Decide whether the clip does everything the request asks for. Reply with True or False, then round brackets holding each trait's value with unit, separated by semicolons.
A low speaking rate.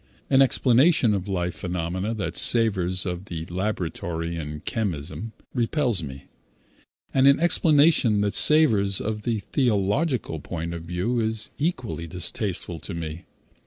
True (130 wpm)